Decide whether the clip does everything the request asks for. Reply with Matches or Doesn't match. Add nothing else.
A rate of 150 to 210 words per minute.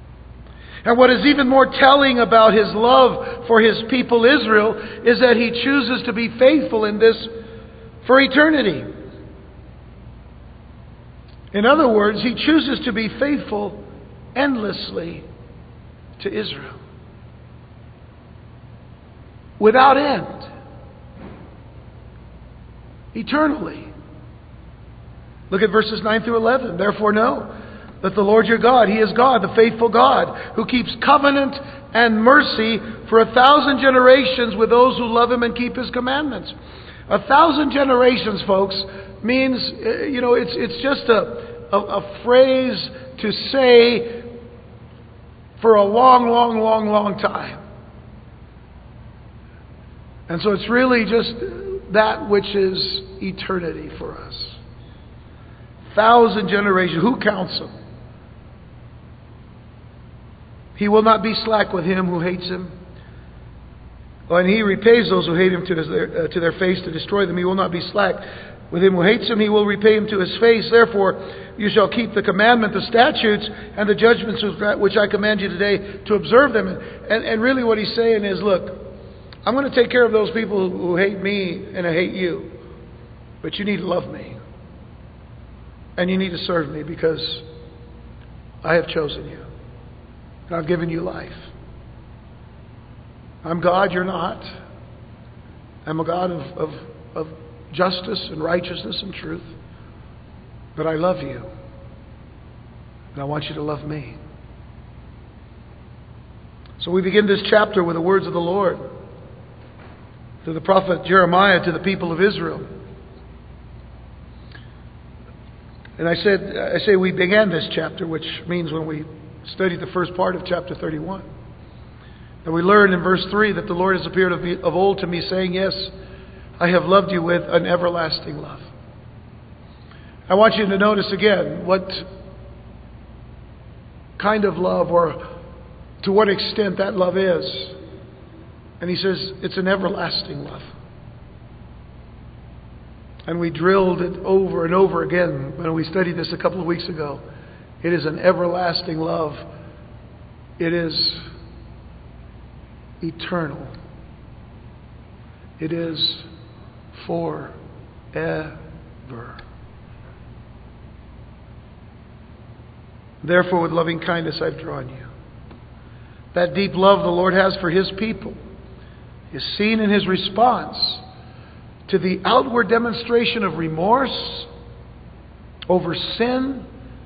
Doesn't match